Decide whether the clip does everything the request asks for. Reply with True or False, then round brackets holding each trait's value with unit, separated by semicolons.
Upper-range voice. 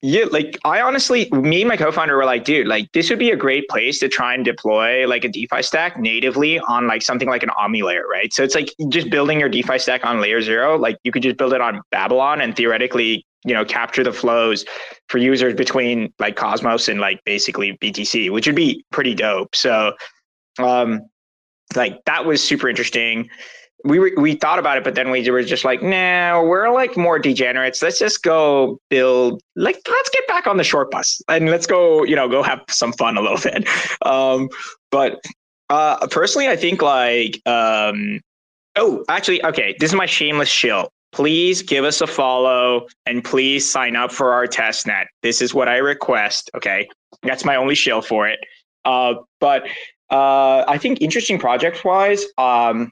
False (130 Hz)